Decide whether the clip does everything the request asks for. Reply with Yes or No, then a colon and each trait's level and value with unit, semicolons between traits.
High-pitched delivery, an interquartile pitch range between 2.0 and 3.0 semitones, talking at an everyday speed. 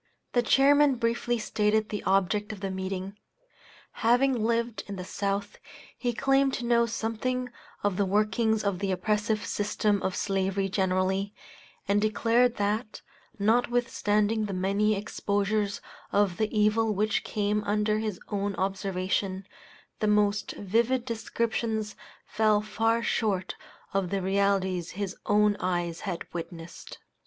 No: high, 210 Hz; narrow, 2.4 semitones; slow, 130 wpm